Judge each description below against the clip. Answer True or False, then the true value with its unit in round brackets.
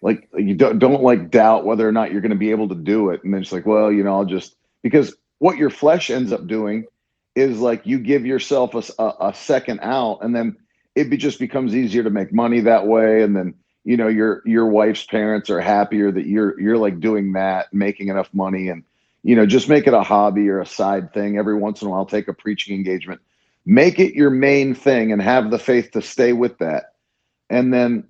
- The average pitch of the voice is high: False (110 Hz)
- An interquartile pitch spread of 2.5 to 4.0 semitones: True (3.4 semitones)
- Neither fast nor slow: False (235 wpm)